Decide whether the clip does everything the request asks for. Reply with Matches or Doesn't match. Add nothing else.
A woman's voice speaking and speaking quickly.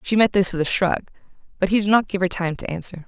Matches